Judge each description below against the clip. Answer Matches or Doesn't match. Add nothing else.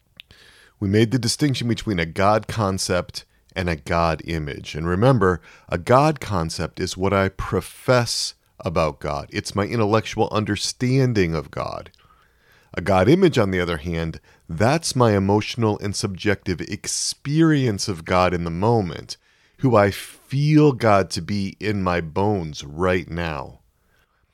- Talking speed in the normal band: Matches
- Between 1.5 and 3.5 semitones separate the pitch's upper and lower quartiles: Doesn't match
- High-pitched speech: Doesn't match